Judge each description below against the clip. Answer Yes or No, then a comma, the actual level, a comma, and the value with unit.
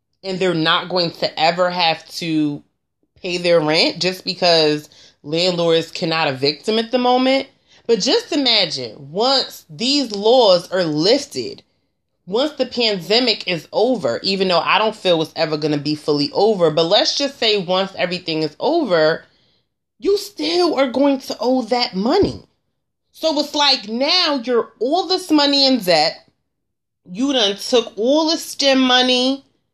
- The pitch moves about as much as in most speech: No, wide, 8.5 semitones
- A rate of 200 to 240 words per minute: No, average, 155 wpm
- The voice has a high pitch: Yes, high, 215 Hz